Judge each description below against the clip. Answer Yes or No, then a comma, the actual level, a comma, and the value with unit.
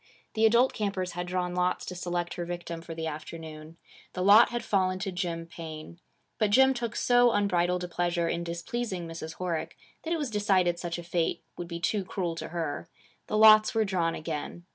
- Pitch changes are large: No, average, 3.4 semitones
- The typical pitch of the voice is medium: Yes, medium, 180 Hz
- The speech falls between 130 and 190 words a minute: No, average, 200 wpm